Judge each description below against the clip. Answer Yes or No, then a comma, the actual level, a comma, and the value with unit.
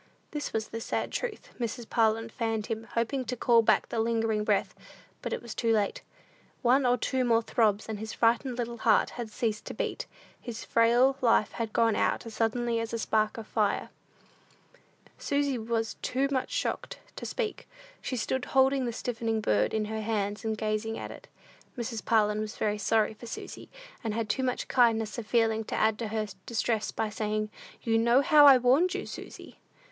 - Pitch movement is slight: Yes, narrow, 2.0 semitones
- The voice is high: Yes, high, 225 Hz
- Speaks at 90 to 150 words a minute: No, average, 195 wpm